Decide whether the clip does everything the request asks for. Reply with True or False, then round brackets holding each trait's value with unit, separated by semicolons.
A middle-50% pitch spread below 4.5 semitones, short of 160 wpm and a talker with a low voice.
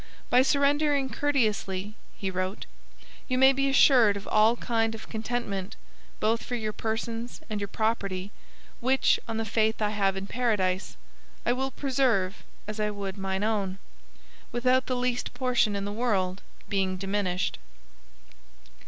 False (4.0 semitones; 145 wpm; 220 Hz)